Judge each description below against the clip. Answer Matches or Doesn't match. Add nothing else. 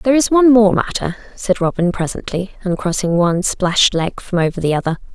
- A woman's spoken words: Matches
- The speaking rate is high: Doesn't match